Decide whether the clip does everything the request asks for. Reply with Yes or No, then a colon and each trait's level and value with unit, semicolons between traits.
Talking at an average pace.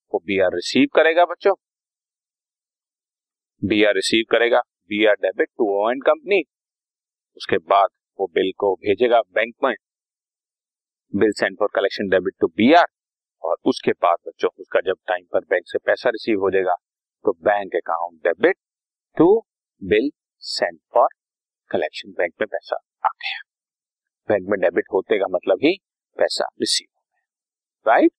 Yes: average, 145 wpm